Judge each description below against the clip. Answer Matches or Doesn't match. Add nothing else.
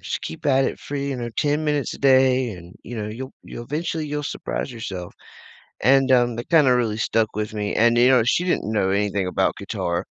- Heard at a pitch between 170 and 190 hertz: Doesn't match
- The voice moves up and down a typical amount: Matches